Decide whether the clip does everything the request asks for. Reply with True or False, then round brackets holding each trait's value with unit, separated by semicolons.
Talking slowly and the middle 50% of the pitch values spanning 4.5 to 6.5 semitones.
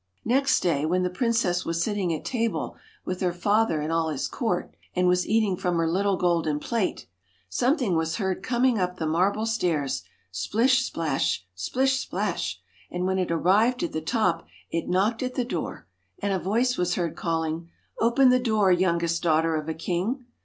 False (185 wpm; 5.3 semitones)